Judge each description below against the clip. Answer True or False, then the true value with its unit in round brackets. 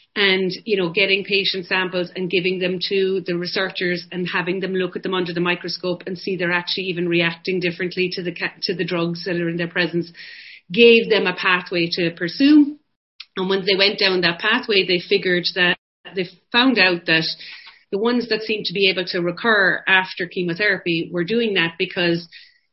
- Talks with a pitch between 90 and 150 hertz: False (185 Hz)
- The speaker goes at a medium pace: True (195 wpm)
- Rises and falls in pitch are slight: True (1.9 semitones)